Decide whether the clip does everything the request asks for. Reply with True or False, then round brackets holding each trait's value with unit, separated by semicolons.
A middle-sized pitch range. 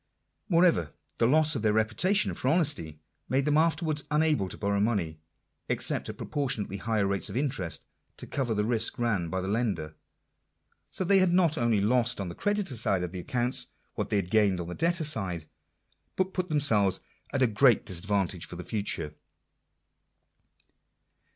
False (7.4 semitones)